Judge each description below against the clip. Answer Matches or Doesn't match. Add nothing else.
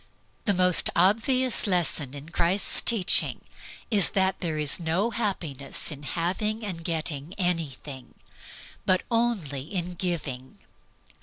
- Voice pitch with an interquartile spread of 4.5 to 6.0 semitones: Matches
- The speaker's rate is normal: Doesn't match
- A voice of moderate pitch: Matches